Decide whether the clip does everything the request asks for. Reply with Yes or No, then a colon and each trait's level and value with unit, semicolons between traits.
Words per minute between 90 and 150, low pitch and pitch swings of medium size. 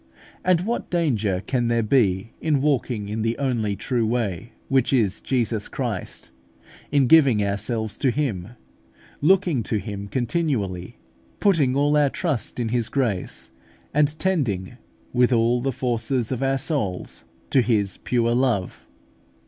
Yes: average, 140 wpm; low, 120 Hz; average, 4.4 semitones